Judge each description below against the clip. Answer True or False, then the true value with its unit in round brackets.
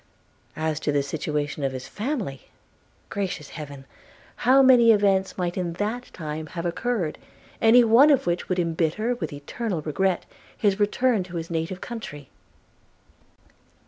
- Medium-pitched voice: True (180 Hz)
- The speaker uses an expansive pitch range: True (6.4 semitones)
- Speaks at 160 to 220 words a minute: False (145 wpm)